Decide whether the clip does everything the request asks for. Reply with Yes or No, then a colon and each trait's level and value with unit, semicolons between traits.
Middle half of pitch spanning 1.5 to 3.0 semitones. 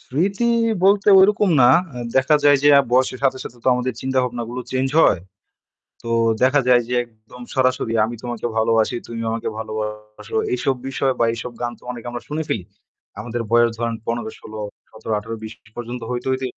Yes: narrow, 2.5 semitones